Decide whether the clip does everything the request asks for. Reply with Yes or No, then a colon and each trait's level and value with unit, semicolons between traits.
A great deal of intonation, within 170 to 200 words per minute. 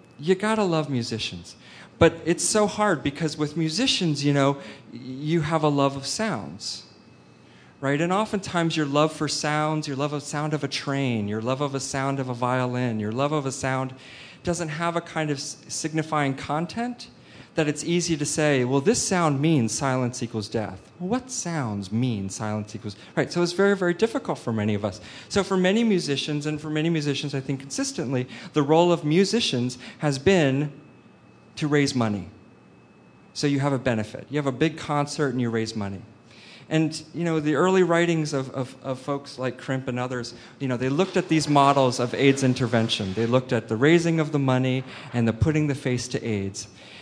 No: average, 4.2 semitones; average, 195 wpm